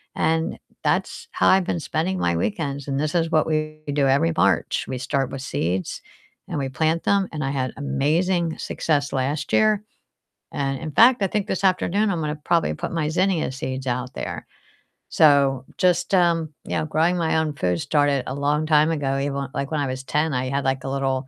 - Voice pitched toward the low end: No, medium, 150 Hz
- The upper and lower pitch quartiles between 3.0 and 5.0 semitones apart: Yes, average, 3.4 semitones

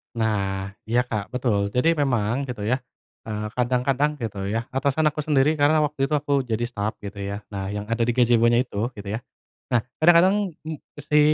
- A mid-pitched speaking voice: No, low, 125 Hz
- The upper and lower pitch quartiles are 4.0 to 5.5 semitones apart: Yes, average, 5.1 semitones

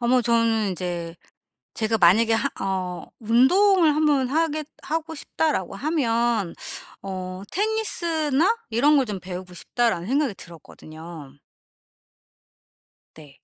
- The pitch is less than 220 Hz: No, high, 230 Hz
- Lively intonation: Yes, wide, 8.5 semitones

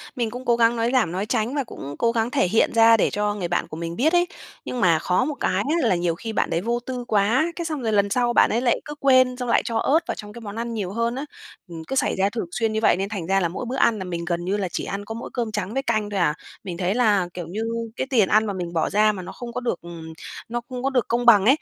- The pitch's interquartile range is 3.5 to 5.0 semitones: Yes, average, 4.3 semitones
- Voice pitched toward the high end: Yes, high, 220 Hz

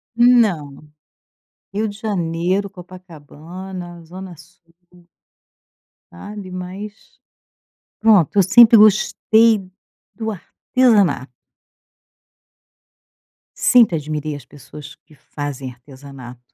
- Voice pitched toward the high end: No, medium, 180 Hz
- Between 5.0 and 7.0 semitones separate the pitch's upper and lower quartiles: Yes, wide, 5.4 semitones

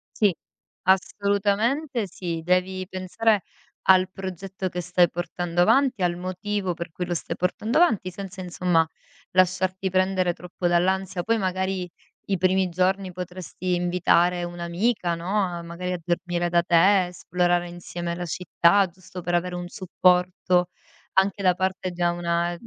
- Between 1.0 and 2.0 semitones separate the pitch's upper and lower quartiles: Yes, narrow, 1.5 semitones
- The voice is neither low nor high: Yes, medium, 180 Hz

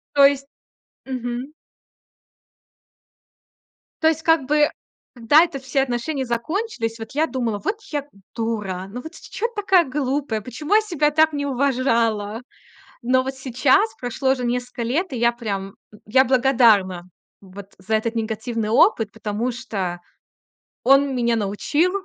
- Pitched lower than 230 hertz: No, very high, 250 Hz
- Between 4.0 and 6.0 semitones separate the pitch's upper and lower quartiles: Yes, average, 4.3 semitones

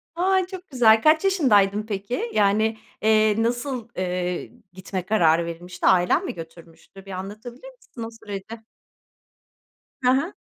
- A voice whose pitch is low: No, high, 215 Hz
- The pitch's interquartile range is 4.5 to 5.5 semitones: Yes, average, 5.1 semitones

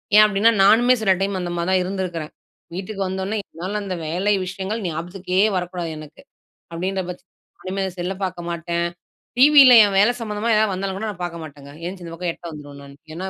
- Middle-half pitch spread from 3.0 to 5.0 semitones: No, narrow, 2.6 semitones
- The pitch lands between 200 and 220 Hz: No, medium, 185 Hz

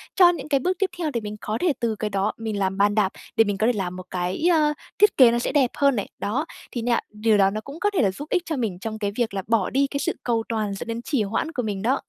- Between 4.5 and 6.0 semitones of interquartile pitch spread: Yes, wide, 5.4 semitones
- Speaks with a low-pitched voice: No, high, 225 Hz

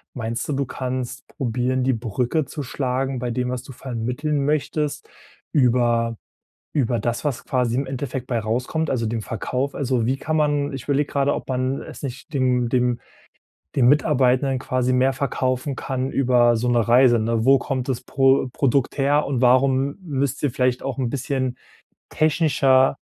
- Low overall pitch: Yes, low, 130 Hz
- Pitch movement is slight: Yes, narrow, 2.0 semitones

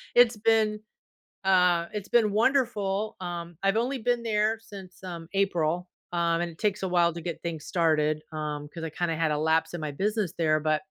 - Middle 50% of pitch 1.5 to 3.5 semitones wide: No, average, 4.5 semitones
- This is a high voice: No, medium, 175 Hz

